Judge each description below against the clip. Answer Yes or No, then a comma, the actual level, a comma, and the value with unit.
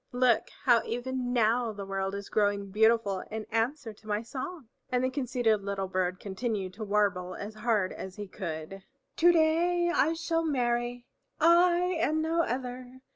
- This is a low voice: No, high, 235 Hz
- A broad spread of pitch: No, average, 4.9 semitones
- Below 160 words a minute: No, average, 165 wpm